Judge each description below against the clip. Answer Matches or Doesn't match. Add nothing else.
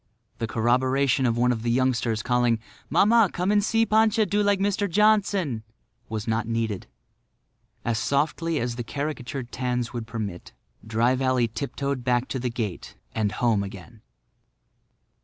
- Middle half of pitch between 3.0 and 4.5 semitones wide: Doesn't match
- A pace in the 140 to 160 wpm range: Matches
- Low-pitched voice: Matches